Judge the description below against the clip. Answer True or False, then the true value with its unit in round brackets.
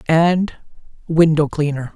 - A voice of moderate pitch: True (160 Hz)